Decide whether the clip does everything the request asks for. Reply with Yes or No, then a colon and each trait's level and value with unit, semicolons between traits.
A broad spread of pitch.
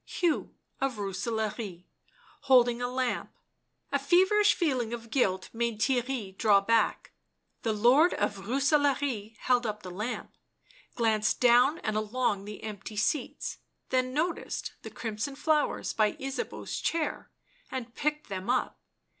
No: average, 4.3 semitones